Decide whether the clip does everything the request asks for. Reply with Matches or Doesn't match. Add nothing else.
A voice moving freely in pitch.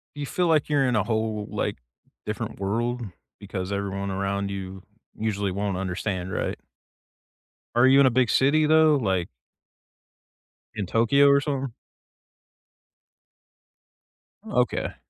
Matches